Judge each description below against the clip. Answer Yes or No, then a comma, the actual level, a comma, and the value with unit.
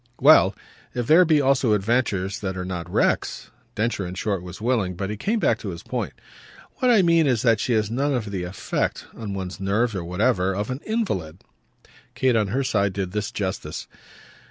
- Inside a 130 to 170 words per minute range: No, average, 200 wpm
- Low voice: Yes, low, 105 Hz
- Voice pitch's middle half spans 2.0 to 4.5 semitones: No, average, 5.1 semitones